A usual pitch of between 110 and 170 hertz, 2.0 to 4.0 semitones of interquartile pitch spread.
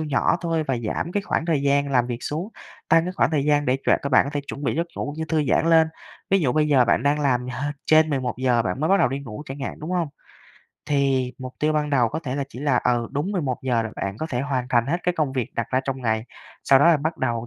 Yes: medium, 140 Hz; average, 3.7 semitones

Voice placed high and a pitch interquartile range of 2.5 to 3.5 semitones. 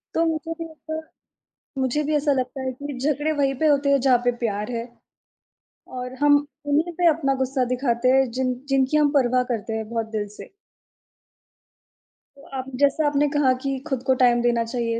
Yes: very high, 265 Hz; average, 2.9 semitones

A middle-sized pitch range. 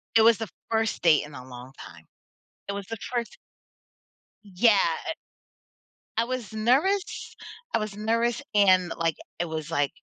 No: wide, 5.8 semitones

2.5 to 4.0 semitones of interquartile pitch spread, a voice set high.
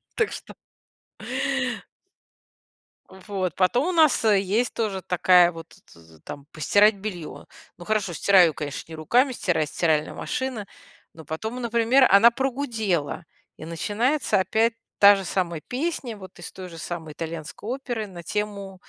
No: average, 5.3 semitones; high, 195 Hz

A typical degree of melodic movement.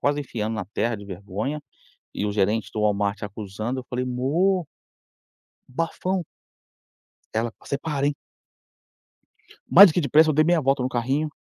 No: wide, 6.1 semitones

